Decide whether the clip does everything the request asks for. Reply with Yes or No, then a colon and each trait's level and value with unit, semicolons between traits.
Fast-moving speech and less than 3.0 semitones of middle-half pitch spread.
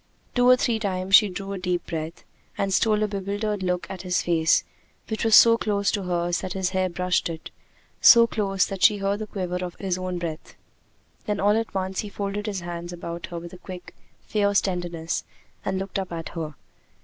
Yes: fast, 210 wpm; narrow, 2.5 semitones